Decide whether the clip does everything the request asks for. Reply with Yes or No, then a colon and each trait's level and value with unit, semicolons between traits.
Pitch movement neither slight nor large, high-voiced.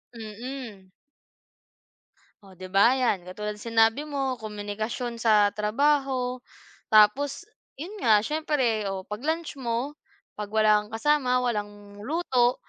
Yes: average, 4.1 semitones; high, 230 Hz